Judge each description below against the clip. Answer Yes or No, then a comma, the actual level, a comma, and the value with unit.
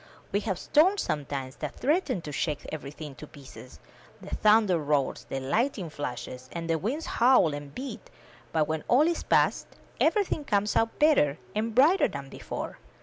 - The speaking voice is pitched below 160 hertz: No, medium, 170 Hz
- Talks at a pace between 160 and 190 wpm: Yes, average, 170 wpm